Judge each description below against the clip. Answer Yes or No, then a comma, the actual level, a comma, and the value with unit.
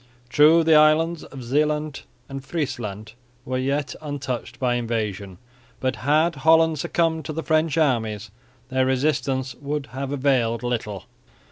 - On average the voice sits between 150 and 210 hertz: No, low, 135 Hz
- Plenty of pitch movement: No, average, 4.0 semitones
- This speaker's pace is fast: No, slow, 135 wpm